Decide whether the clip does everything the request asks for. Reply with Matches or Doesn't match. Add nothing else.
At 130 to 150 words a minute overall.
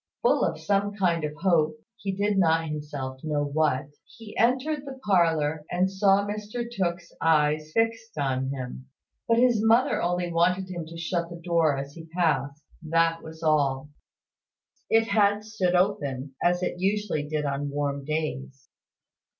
Doesn't match